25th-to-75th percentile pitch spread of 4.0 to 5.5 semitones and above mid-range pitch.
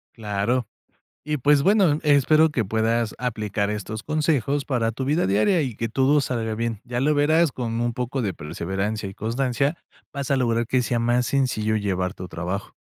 No: average, 4.4 semitones; low, 120 Hz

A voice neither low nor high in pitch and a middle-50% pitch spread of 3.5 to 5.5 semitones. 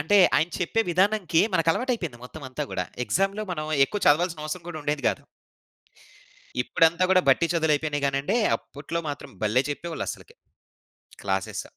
Yes: medium, 160 Hz; average, 3.9 semitones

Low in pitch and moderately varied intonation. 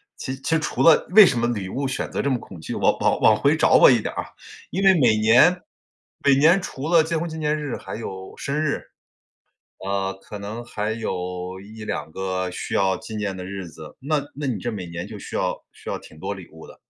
No: low, 110 Hz; wide, 7.2 semitones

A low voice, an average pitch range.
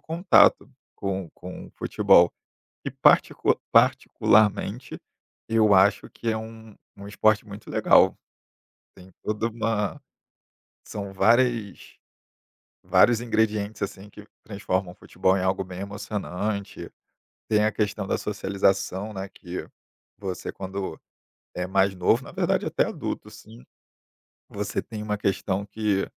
No: low, 100 Hz; narrow, 2.1 semitones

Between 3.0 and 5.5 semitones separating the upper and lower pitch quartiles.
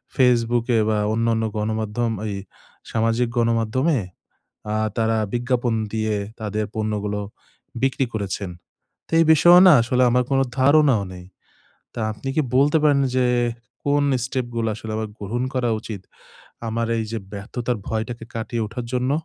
No: narrow, 2.6 semitones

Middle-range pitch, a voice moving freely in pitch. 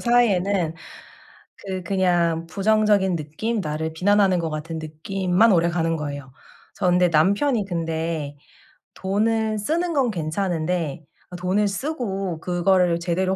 No: medium, 180 Hz; average, 3.7 semitones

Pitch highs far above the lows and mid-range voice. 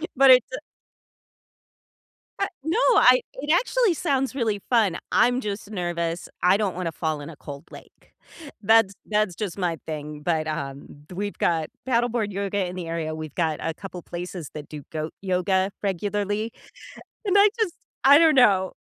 No: wide, 6.1 semitones; high, 195 Hz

